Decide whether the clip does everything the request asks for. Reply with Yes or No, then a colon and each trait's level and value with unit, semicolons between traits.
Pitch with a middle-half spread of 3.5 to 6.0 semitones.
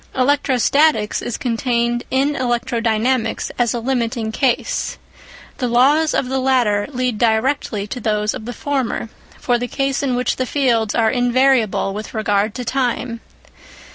No: average, 2.7 semitones